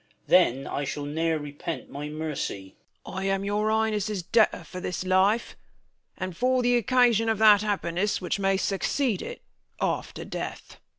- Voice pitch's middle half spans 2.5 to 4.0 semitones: No, average, 5.0 semitones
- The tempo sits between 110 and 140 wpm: No, average, 160 wpm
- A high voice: Yes, high, 195 Hz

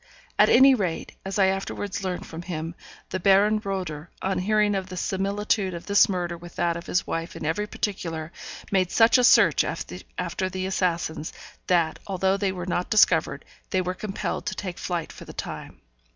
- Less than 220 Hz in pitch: Yes, medium, 185 Hz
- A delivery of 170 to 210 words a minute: Yes, average, 190 wpm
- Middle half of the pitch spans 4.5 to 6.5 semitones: No, narrow, 2.4 semitones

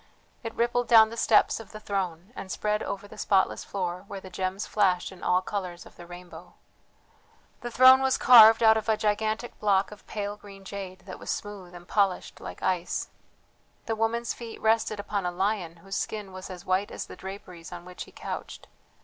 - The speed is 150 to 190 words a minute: No, average, 200 wpm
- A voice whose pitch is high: Yes, high, 200 Hz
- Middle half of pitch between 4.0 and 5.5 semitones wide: No, average, 2.9 semitones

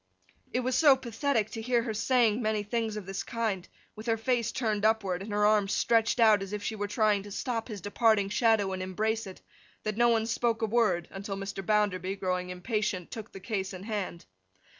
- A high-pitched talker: Yes, high, 215 Hz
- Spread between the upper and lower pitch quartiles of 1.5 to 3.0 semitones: Yes, narrow, 2.6 semitones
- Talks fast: Yes, fast, 210 wpm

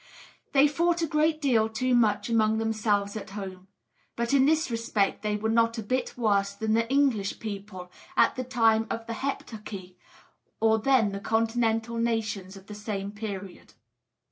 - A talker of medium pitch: No, high, 220 Hz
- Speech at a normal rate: Yes, average, 170 wpm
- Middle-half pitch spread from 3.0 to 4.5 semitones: No, narrow, 2.6 semitones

